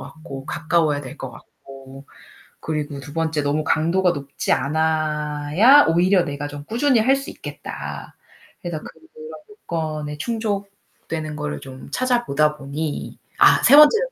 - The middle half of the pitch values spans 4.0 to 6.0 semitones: Yes, average, 5.1 semitones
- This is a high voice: No, medium, 155 Hz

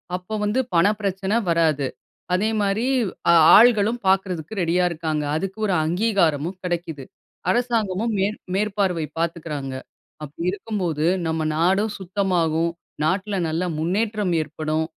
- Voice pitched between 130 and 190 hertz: Yes, medium, 185 Hz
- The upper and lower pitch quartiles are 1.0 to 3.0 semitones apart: No, average, 4.1 semitones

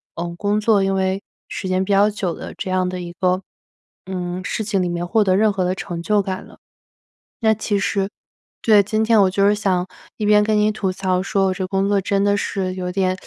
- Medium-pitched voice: No, high, 195 Hz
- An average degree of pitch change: No, narrow, 1.9 semitones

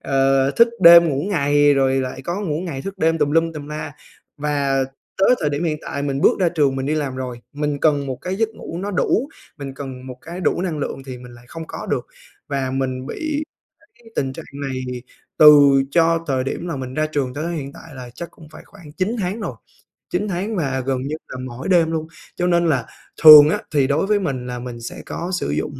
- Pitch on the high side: No, medium, 145 Hz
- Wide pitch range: No, average, 4.1 semitones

